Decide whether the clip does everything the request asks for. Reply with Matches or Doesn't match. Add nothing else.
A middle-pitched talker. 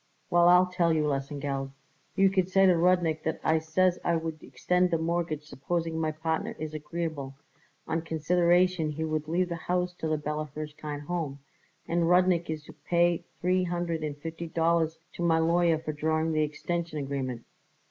Matches